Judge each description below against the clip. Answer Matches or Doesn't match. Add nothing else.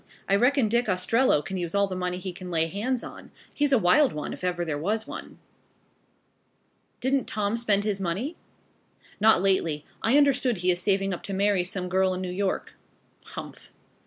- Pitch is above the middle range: Matches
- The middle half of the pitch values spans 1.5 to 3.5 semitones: Doesn't match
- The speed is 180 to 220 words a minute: Matches